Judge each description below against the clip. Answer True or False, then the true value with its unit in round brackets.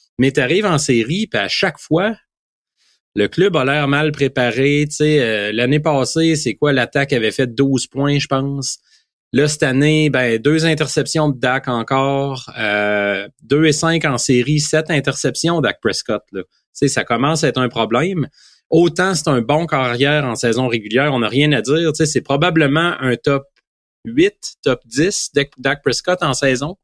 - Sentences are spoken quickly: False (180 wpm)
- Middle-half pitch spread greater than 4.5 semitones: False (3.4 semitones)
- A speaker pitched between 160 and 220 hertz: False (140 Hz)